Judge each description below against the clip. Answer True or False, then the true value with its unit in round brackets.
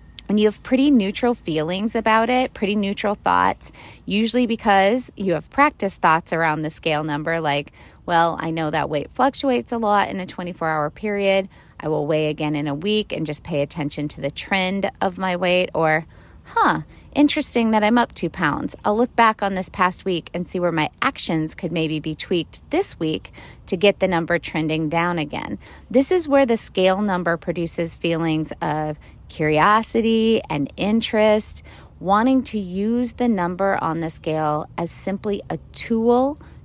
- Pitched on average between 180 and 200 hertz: True (185 Hz)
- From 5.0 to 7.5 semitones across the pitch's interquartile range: True (5.6 semitones)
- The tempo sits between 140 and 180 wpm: True (175 wpm)